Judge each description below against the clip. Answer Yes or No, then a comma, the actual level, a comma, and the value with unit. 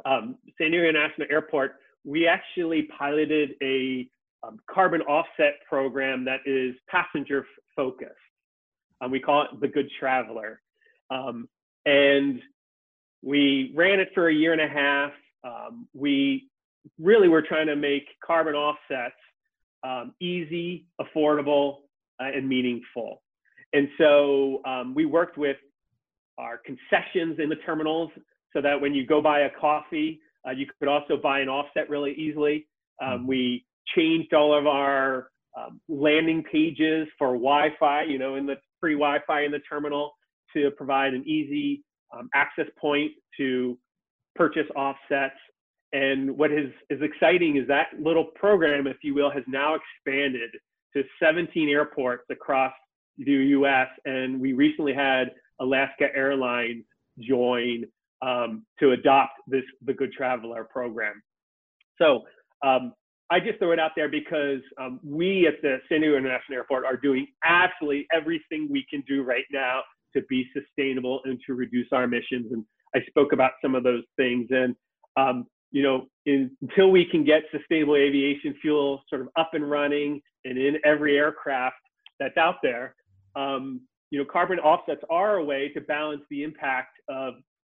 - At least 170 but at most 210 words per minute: No, average, 155 wpm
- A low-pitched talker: No, medium, 145 Hz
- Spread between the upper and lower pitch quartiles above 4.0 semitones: No, average, 2.7 semitones